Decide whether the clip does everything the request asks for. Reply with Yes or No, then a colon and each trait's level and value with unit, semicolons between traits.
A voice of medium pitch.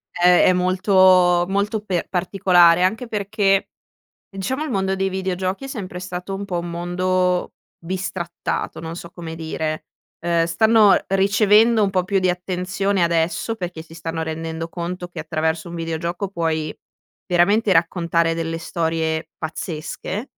Yes: medium, 180 Hz